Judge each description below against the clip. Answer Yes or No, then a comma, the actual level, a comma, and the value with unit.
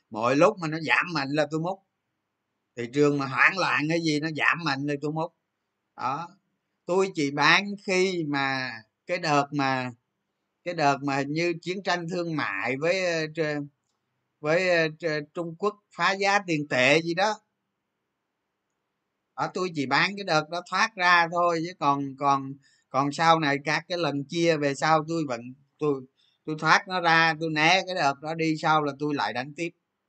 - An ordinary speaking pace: Yes, average, 180 wpm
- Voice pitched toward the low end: No, medium, 160 Hz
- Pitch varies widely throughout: No, average, 3.6 semitones